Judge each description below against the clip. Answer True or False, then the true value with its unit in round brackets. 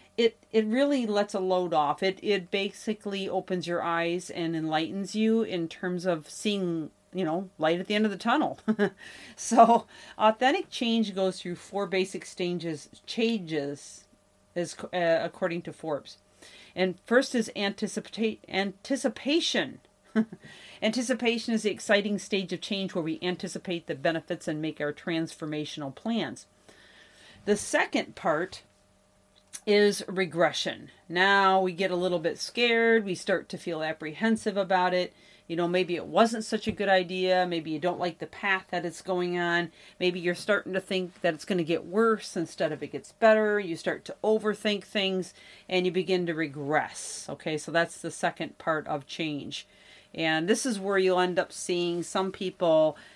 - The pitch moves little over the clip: False (3.6 semitones)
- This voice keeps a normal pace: True (165 wpm)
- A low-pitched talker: False (185 Hz)